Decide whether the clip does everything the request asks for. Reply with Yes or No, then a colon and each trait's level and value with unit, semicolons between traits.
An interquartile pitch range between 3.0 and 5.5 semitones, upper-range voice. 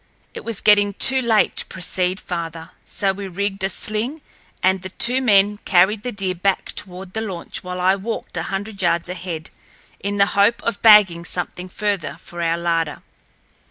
No: narrow, 2.6 semitones; high, 195 Hz